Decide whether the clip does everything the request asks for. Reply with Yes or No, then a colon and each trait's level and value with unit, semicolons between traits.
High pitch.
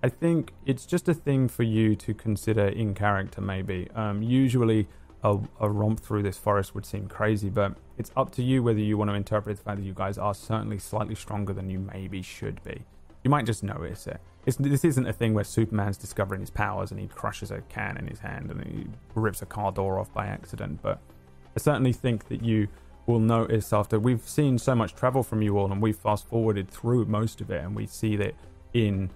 No: low, 105 Hz